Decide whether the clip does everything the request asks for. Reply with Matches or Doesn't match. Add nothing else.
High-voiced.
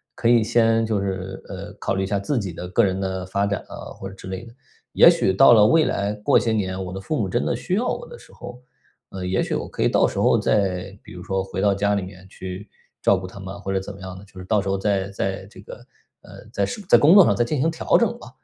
Doesn't match